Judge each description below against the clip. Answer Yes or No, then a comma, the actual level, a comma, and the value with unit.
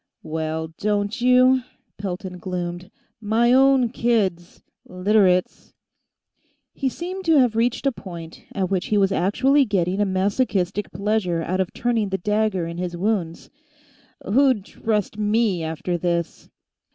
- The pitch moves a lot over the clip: No, average, 4.4 semitones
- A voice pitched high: Yes, high, 200 Hz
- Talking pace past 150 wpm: No, slow, 135 wpm